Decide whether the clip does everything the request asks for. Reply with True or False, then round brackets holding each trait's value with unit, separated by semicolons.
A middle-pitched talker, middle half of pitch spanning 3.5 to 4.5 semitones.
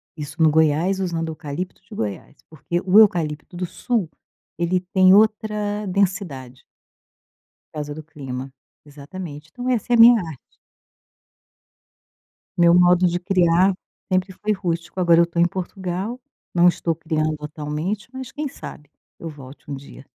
True (175 Hz; 3.9 semitones)